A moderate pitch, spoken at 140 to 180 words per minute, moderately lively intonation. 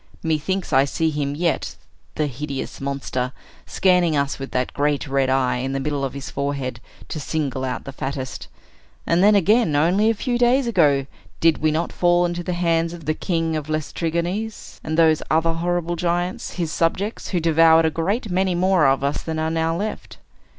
No: medium, 160 Hz; average, 190 wpm; average, 3.8 semitones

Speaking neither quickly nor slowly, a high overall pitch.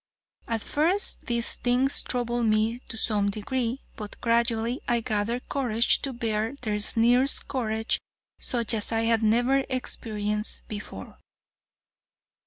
No: slow, 125 wpm; high, 230 Hz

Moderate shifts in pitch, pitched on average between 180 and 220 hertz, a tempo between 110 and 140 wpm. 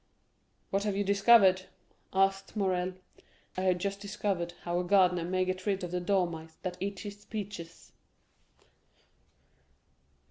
No: narrow, 1.9 semitones; high, 190 Hz; slow, 135 wpm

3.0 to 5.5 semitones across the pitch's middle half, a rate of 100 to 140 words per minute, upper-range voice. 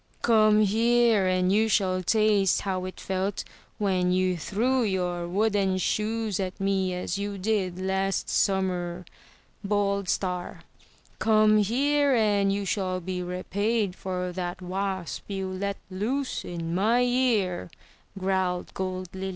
No: narrow, 2.5 semitones; slow, 135 wpm; high, 195 Hz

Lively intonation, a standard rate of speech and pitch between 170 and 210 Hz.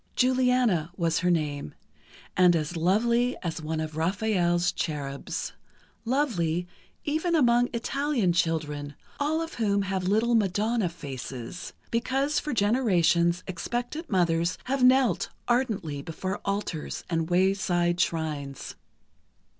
No: wide, 6.6 semitones; slow, 110 wpm; medium, 185 Hz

